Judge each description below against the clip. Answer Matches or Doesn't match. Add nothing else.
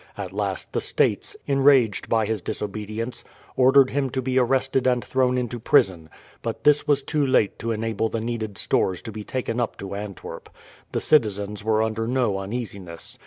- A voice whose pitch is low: Matches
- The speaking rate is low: Doesn't match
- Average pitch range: Matches